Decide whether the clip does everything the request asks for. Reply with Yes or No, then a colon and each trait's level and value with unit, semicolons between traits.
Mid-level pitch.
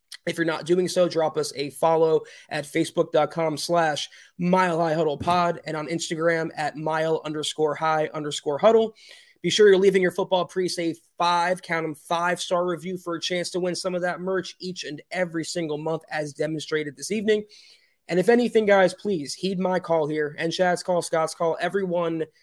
Yes: medium, 170 Hz